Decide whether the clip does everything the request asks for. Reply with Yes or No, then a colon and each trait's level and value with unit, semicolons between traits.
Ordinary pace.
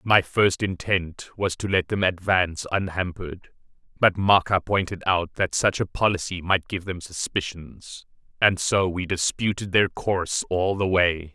Yes: average, 160 wpm